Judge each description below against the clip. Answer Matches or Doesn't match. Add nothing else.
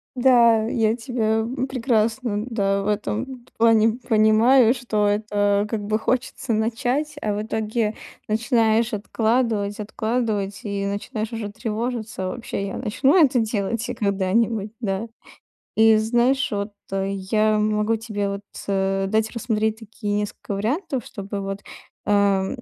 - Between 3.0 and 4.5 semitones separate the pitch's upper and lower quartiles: Doesn't match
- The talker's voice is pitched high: Matches